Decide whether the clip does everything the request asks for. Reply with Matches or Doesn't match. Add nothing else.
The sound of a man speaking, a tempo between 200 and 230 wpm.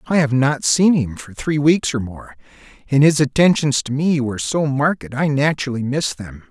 Matches